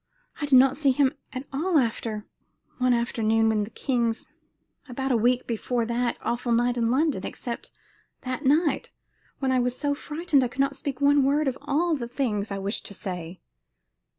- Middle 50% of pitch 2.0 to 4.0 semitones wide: Yes, average, 3.2 semitones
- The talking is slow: No, average, 185 wpm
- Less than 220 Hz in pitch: No, very high, 250 Hz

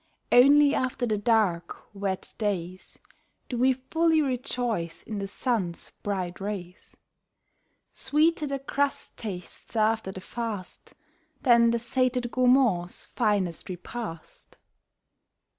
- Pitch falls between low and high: No, high, 225 Hz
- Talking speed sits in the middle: No, slow, 110 wpm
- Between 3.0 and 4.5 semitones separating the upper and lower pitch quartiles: No, average, 5.0 semitones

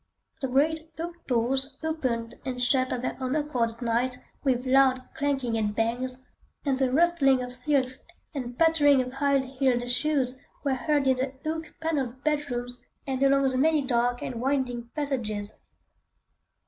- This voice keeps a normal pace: Yes, average, 160 wpm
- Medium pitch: No, very high, 260 Hz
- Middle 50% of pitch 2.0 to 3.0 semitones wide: Yes, narrow, 2.5 semitones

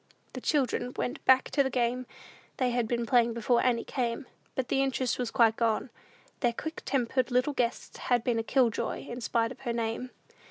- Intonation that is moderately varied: No, narrow, 1.7 semitones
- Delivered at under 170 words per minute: No, average, 200 wpm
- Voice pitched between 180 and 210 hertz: No, high, 245 Hz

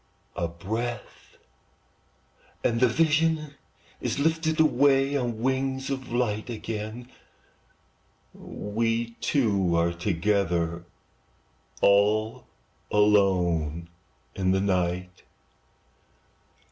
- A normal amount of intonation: No, wide, 6.2 semitones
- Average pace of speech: No, slow, 85 wpm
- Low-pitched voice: Yes, low, 110 Hz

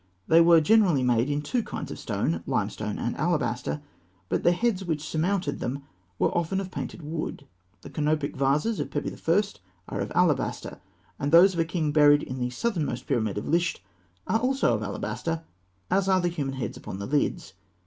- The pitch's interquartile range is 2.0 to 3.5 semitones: No, average, 4.4 semitones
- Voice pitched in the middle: Yes, medium, 155 Hz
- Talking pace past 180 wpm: Yes, average, 190 wpm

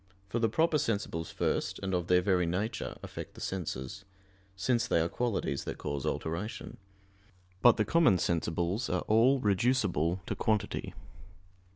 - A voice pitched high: No, very low, 95 Hz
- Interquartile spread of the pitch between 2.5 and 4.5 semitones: No, average, 5.0 semitones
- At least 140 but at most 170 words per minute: Yes, average, 150 wpm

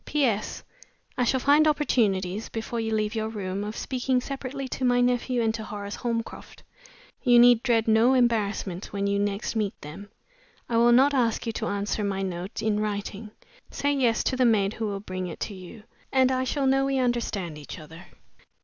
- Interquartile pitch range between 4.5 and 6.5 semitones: No, average, 3.7 semitones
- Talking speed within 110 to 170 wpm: No, average, 195 wpm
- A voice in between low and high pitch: No, high, 225 Hz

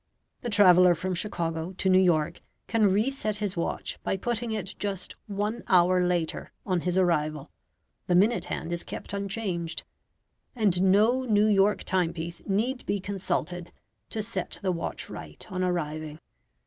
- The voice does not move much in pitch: No, average, 3.2 semitones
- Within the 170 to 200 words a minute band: No, average, 150 wpm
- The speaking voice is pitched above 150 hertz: Yes, medium, 185 Hz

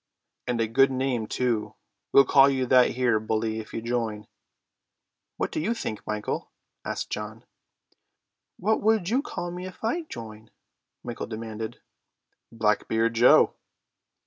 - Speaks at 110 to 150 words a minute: Yes, average, 140 wpm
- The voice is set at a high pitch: No, low, 115 Hz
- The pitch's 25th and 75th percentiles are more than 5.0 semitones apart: No, average, 3.8 semitones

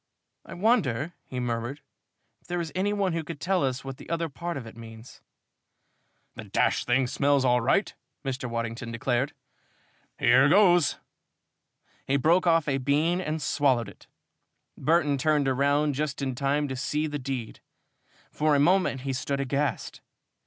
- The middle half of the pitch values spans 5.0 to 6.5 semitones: No, average, 3.8 semitones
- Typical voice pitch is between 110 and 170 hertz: Yes, medium, 140 Hz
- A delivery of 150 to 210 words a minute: Yes, average, 165 wpm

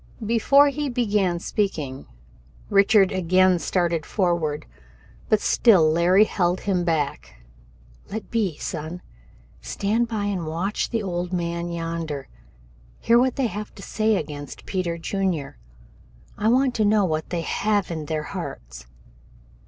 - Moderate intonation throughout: Yes, average, 4.3 semitones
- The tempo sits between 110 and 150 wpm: Yes, slow, 135 wpm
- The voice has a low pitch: No, medium, 185 Hz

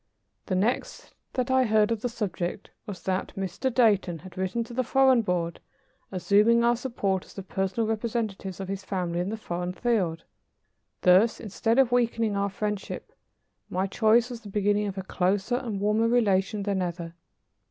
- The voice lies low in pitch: No, high, 205 Hz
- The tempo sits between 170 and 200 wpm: Yes, average, 175 wpm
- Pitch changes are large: No, average, 3.6 semitones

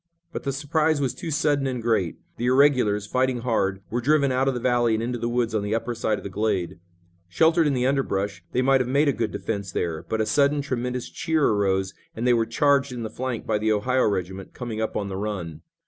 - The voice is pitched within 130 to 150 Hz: No, low, 120 Hz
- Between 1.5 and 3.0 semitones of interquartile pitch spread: No, average, 4.4 semitones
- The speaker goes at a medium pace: No, fast, 240 wpm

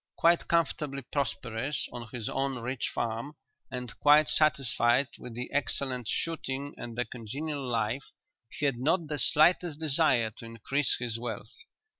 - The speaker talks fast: No, average, 145 wpm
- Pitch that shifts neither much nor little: Yes, average, 3.7 semitones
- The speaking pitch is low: Yes, low, 130 Hz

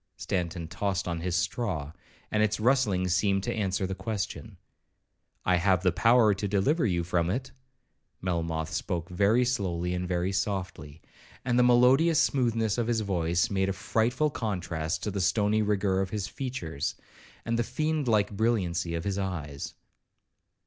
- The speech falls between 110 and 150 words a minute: No, average, 160 wpm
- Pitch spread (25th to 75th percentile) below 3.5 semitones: No, average, 4.3 semitones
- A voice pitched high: No, very low, 95 Hz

